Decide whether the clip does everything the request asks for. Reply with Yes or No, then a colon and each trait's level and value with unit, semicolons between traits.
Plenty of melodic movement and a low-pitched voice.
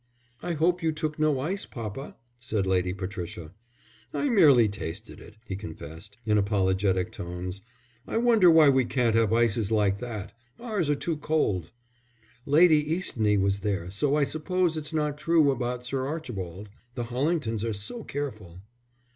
Yes: wide, 7.5 semitones; low, 120 Hz